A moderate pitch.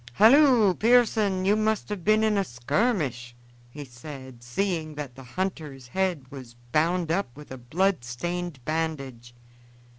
Yes: medium, 160 Hz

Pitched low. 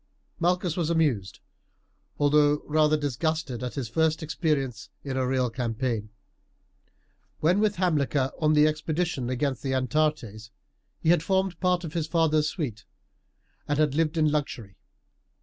No: medium, 150 Hz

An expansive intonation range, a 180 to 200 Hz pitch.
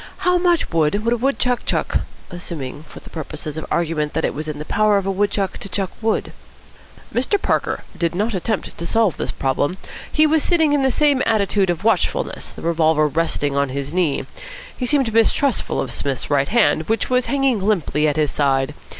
Yes: wide, 7.5 semitones; high, 190 Hz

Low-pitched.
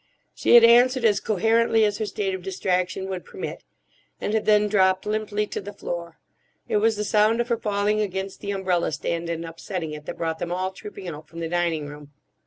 No: high, 195 Hz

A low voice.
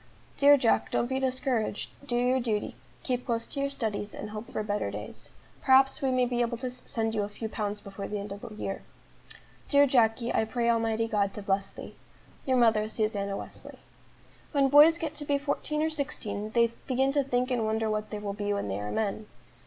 No: high, 230 Hz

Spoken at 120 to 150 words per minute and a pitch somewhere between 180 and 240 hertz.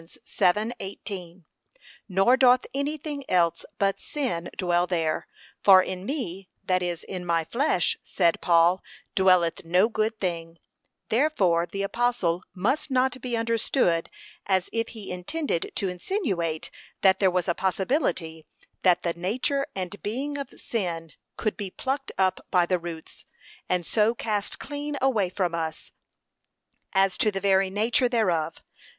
Yes: average, 145 wpm; high, 190 Hz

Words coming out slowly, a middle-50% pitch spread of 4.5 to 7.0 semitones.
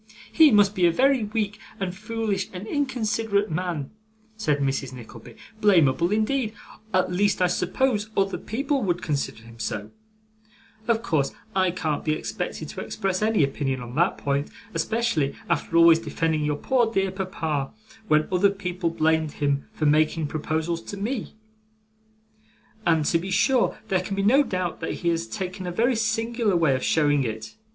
No: average, 165 wpm; wide, 5.5 semitones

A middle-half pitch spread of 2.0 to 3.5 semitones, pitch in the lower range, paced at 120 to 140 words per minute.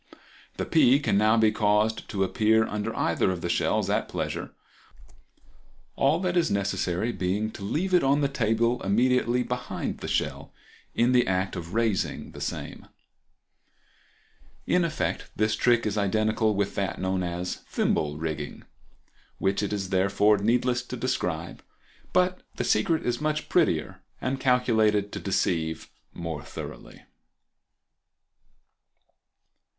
No: average, 4.5 semitones; low, 110 Hz; slow, 135 wpm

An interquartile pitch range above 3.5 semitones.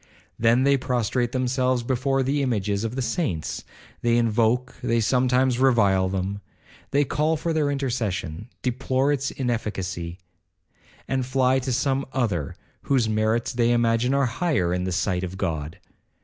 Yes: average, 4.2 semitones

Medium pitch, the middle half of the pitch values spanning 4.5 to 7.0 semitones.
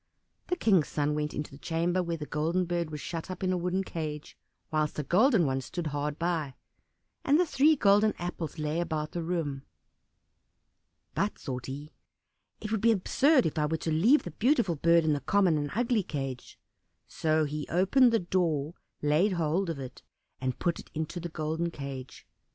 No: medium, 165 Hz; average, 3.6 semitones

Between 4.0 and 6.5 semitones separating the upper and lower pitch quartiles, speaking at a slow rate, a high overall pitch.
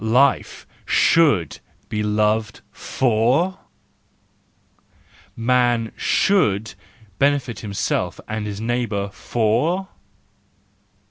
No: average, 4.4 semitones; slow, 70 wpm; low, 115 Hz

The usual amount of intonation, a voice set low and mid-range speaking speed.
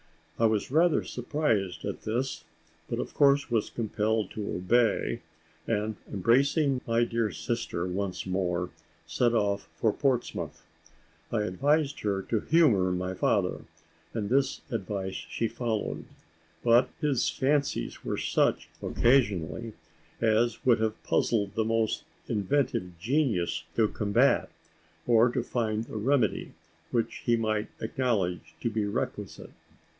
No: average, 3.5 semitones; low, 115 Hz; slow, 130 wpm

